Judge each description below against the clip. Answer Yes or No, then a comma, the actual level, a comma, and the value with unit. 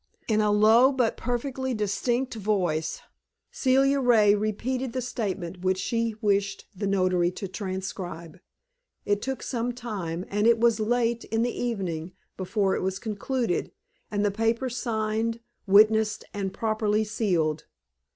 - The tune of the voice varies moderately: Yes, average, 3.4 semitones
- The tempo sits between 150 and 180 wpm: No, average, 140 wpm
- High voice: Yes, high, 215 Hz